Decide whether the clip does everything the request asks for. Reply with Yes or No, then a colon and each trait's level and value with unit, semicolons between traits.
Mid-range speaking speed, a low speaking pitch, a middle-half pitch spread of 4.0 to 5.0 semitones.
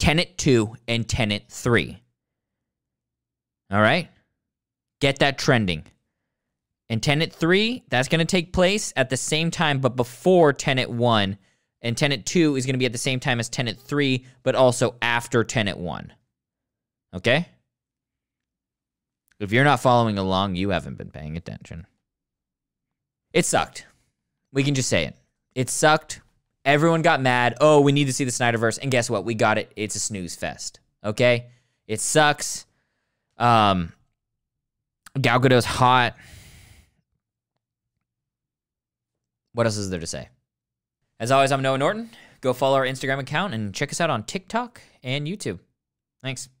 Yes: average, 150 wpm; low, 125 Hz; average, 4.4 semitones